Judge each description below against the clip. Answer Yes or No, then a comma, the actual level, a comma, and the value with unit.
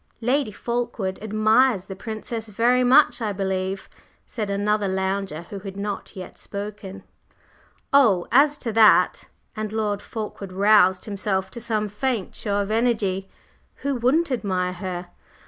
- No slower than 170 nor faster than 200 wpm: No, average, 140 wpm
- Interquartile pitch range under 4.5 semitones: Yes, average, 3.3 semitones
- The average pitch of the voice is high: Yes, high, 210 Hz